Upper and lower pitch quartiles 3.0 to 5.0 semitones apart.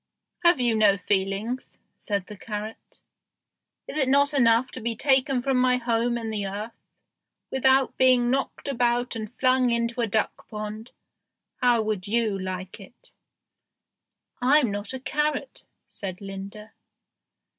Yes: average, 3.5 semitones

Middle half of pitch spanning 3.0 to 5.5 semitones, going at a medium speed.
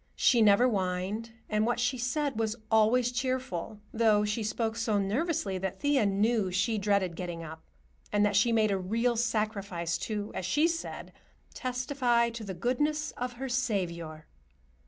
Yes: average, 3.8 semitones; average, 160 wpm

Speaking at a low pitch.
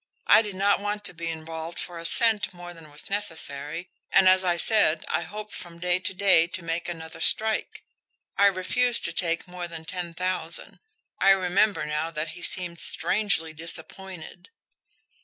No: medium, 175 Hz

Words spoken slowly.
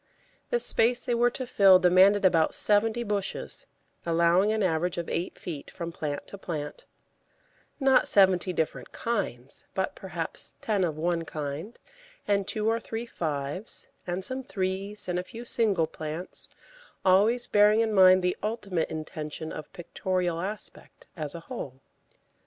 No: average, 150 wpm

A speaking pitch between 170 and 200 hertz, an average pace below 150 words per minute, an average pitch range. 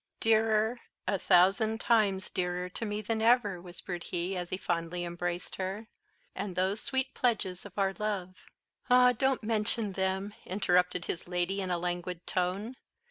No: high, 190 Hz; average, 155 wpm; average, 3.4 semitones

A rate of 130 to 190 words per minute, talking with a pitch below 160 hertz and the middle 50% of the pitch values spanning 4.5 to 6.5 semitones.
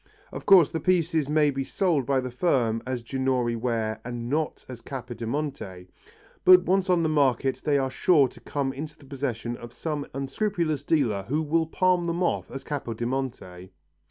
Yes: average, 175 wpm; medium, 140 Hz; average, 4.8 semitones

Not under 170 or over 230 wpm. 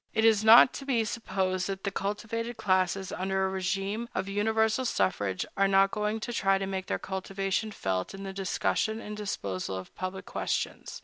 Yes: average, 185 wpm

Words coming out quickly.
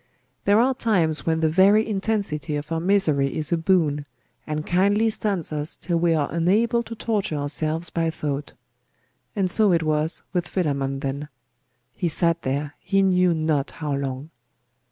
No: average, 165 wpm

